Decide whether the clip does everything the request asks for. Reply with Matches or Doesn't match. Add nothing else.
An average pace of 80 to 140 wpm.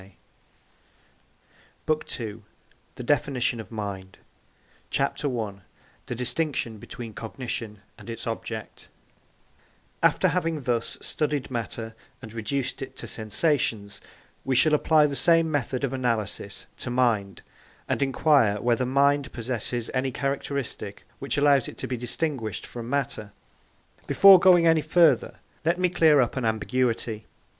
Matches